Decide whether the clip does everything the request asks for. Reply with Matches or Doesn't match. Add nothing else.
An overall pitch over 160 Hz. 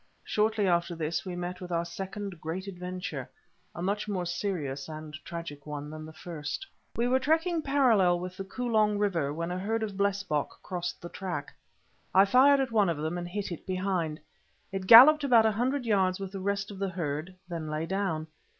Matches